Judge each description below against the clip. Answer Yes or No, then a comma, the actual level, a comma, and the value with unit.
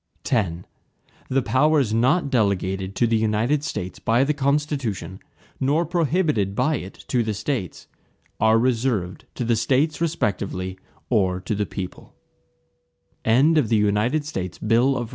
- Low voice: Yes, low, 115 Hz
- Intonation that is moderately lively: No, wide, 6.1 semitones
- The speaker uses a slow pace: Yes, slow, 115 wpm